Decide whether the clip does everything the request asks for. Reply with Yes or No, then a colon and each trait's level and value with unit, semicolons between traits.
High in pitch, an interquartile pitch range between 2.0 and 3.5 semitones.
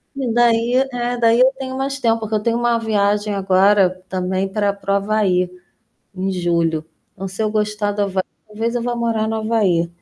Yes: high, 215 Hz; average, 3.1 semitones